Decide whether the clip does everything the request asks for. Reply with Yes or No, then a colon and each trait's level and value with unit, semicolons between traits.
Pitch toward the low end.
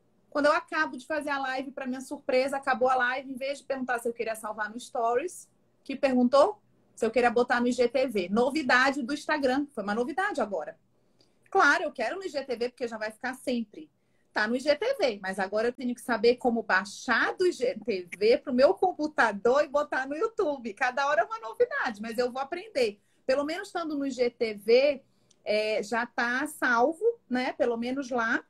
No: very high, 260 Hz